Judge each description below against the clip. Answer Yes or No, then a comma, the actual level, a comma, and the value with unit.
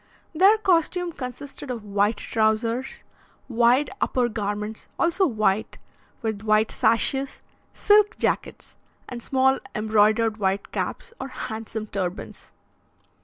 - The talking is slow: Yes, slow, 110 wpm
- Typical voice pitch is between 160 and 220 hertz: No, high, 230 Hz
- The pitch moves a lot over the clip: No, average, 4.1 semitones